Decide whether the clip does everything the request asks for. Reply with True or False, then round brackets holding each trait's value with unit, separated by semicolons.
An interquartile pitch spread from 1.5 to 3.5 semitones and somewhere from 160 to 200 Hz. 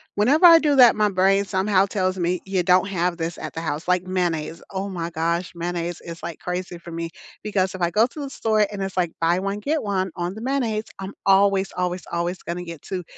True (2.7 semitones; 185 Hz)